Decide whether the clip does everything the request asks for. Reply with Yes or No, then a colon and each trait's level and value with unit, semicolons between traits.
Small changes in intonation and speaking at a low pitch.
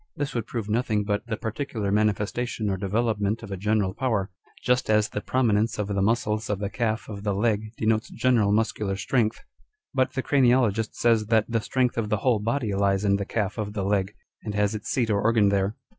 Yes: narrow, 2.3 semitones; low, 110 Hz